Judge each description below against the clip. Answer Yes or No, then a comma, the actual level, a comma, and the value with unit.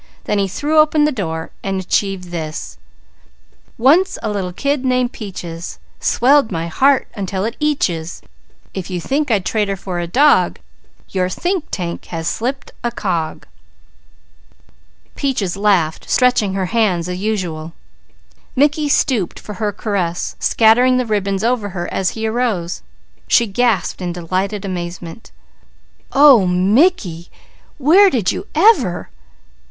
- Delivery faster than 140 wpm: No, slow, 135 wpm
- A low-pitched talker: No, high, 205 Hz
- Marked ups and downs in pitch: Yes, wide, 6.0 semitones